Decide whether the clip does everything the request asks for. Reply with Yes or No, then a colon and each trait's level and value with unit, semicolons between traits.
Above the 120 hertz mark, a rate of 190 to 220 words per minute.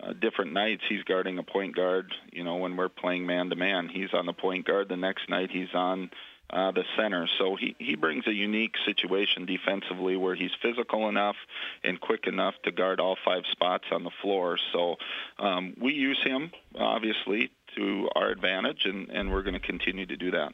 No: very low, 95 Hz; average, 200 wpm